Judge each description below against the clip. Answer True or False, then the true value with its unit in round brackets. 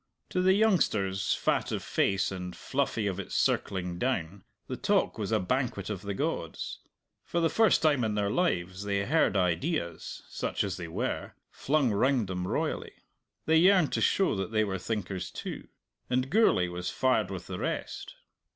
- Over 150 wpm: True (175 wpm)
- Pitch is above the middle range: False (105 Hz)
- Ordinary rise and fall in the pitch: False (7.3 semitones)